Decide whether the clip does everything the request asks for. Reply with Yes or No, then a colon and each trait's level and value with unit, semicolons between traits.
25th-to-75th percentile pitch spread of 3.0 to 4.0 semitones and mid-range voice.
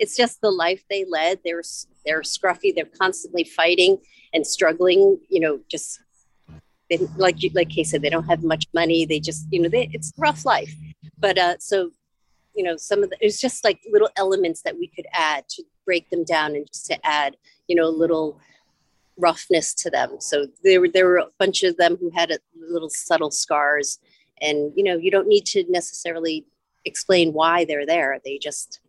Yes: average, 3.4 semitones; medium, 170 Hz